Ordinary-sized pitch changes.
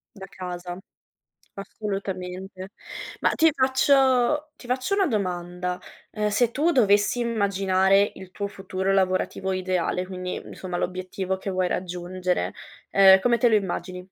Yes: average, 3.0 semitones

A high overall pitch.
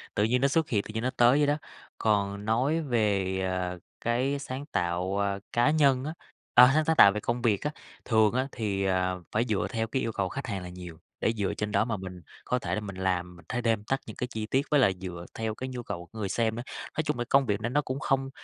No: low, 110 Hz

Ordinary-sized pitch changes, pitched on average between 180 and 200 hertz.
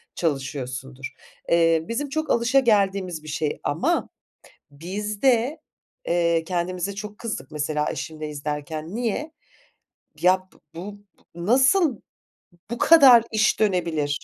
No: wide, 6.9 semitones; medium, 185 Hz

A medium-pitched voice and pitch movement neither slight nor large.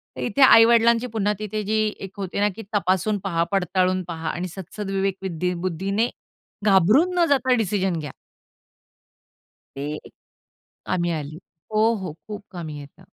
No: high, 195 Hz; average, 3.5 semitones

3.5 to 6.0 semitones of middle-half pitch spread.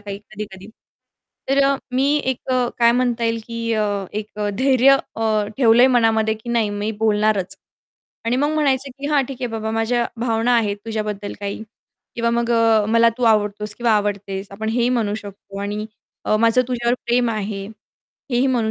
No: narrow, 2.5 semitones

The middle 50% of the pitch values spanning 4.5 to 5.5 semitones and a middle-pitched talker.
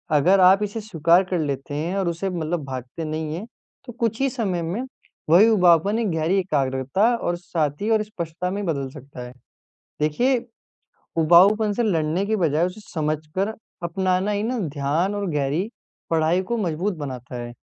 Yes: average, 4.8 semitones; medium, 175 Hz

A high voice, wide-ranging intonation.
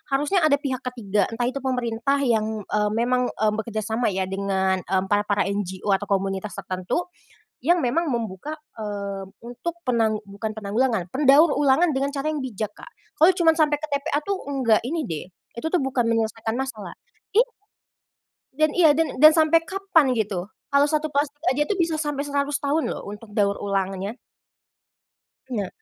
Yes: high, 245 Hz; wide, 6.2 semitones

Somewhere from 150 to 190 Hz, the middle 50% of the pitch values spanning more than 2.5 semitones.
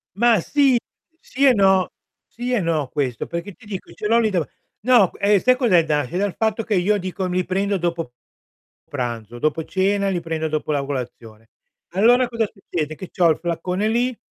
Yes: medium, 185 Hz; average, 5.3 semitones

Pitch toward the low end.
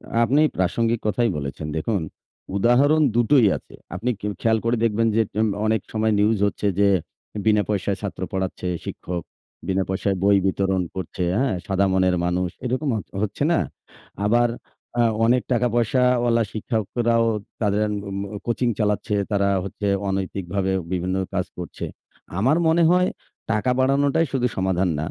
Yes: low, 105 Hz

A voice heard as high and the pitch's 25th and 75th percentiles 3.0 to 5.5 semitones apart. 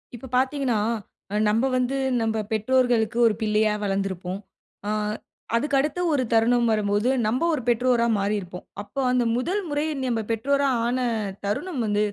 Yes: high, 235 Hz; average, 3.7 semitones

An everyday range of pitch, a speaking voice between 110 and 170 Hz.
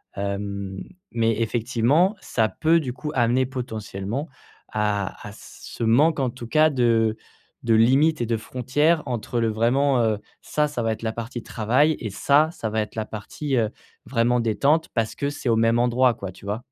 Yes: average, 3.5 semitones; low, 120 Hz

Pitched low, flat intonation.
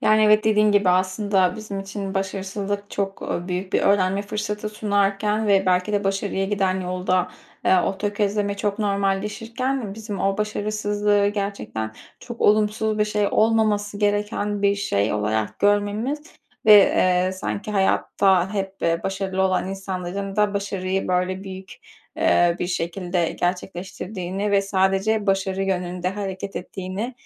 No: high, 200 Hz; narrow, 1.7 semitones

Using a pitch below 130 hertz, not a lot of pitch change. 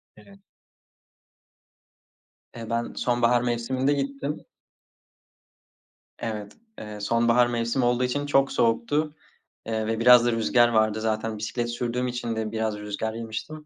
Yes: low, 120 Hz; narrow, 2.0 semitones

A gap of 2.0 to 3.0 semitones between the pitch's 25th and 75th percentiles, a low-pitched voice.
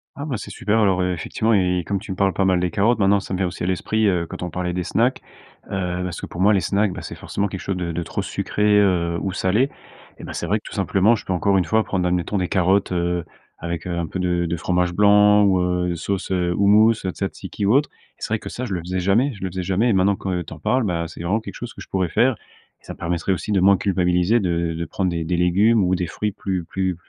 Yes: narrow, 2.6 semitones; very low, 95 Hz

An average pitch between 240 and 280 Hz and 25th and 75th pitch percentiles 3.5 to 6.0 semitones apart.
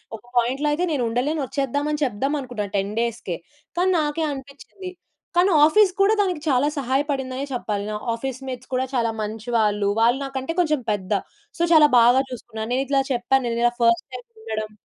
Yes: very high, 260 Hz; average, 4.0 semitones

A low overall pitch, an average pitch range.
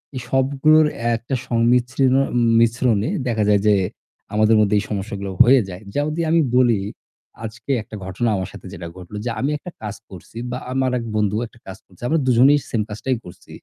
Yes: low, 115 Hz; average, 3.8 semitones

